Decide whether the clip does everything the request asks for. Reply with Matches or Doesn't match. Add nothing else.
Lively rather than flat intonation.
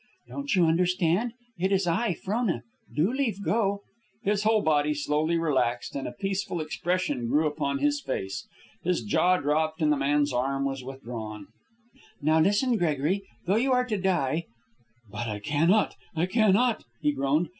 Matches